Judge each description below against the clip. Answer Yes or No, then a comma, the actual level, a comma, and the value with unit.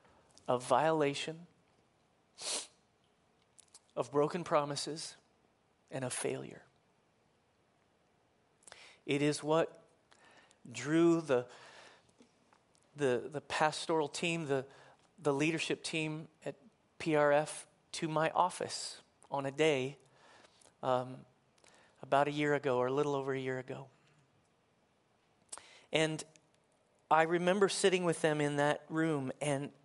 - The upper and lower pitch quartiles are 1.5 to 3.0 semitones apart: Yes, average, 2.7 semitones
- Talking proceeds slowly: Yes, slow, 105 wpm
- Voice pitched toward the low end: No, medium, 145 Hz